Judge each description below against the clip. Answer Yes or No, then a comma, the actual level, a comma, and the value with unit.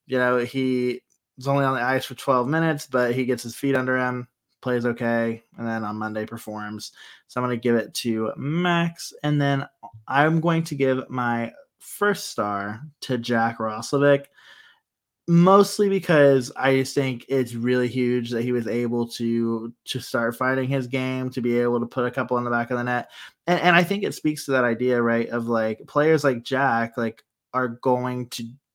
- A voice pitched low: Yes, low, 125 Hz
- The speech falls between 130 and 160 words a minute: No, average, 195 wpm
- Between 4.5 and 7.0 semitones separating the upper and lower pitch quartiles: No, average, 2.8 semitones